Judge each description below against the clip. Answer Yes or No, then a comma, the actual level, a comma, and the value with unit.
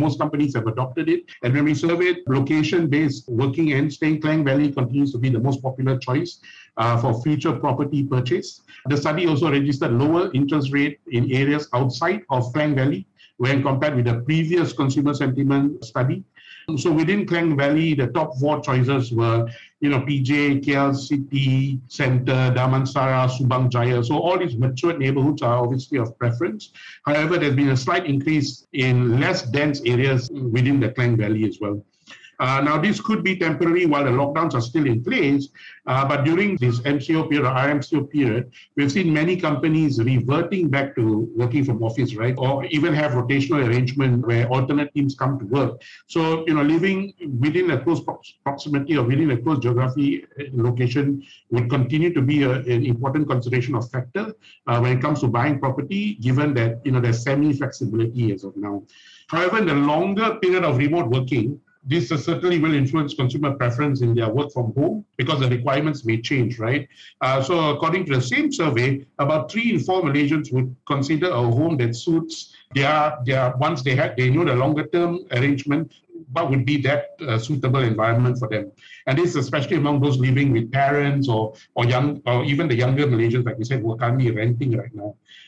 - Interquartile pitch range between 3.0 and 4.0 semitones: Yes, average, 3.5 semitones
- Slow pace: No, average, 185 wpm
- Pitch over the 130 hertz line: Yes, medium, 140 Hz